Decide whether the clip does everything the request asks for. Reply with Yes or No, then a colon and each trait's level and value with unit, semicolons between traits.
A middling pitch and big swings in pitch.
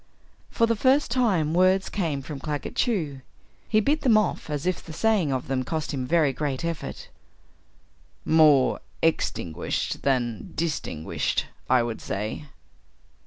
Yes: medium, 155 Hz; wide, 6.1 semitones